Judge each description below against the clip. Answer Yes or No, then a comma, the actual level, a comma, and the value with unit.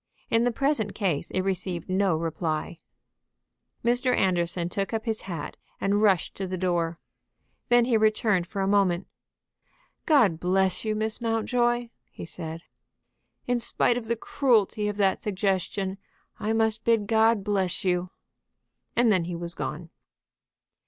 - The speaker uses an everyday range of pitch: Yes, average, 3.9 semitones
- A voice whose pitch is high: Yes, high, 200 Hz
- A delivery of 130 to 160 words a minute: Yes, average, 145 wpm